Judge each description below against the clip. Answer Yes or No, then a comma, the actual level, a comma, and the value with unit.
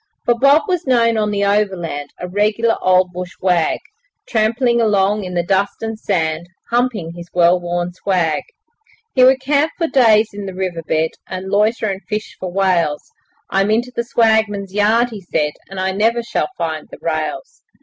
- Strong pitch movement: No, average, 4.3 semitones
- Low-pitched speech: No, high, 200 Hz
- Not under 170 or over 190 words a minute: Yes, average, 180 wpm